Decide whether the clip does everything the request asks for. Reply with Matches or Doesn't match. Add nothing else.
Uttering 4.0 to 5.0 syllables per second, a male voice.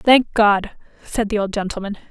Doesn't match